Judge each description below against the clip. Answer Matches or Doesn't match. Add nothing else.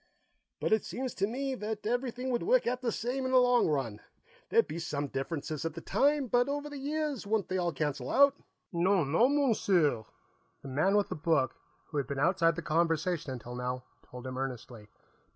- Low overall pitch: Doesn't match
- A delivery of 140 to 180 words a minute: Doesn't match